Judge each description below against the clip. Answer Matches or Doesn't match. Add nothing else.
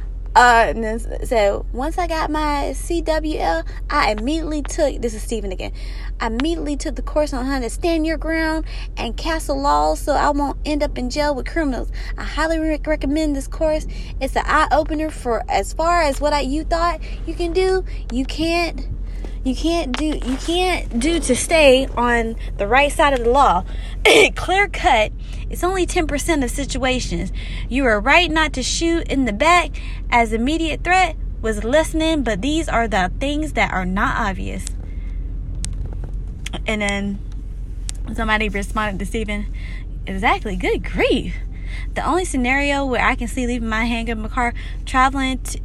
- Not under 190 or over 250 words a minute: Doesn't match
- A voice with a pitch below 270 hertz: Doesn't match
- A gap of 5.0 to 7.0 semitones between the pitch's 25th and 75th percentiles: Matches